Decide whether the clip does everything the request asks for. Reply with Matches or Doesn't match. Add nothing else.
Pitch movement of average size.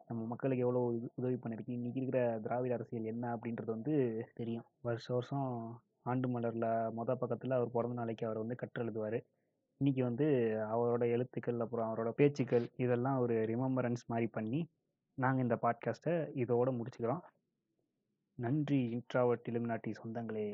Doesn't match